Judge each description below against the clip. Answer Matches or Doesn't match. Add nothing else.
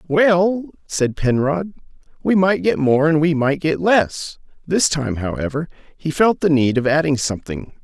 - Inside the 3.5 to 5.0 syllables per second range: Matches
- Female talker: Doesn't match